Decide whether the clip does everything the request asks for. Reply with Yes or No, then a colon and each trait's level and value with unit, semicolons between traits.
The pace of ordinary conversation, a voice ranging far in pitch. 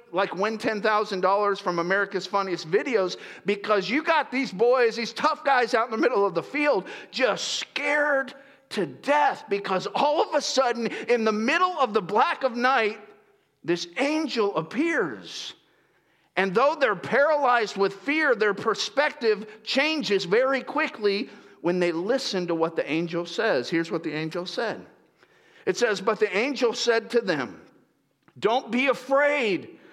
Yes: average, 155 wpm; wide, 6.0 semitones